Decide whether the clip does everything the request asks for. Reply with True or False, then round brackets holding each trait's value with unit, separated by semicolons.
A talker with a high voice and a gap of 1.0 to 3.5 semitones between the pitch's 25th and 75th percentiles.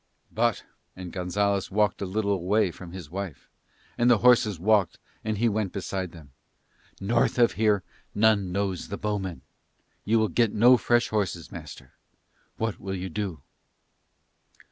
False (100 Hz; 2.9 semitones)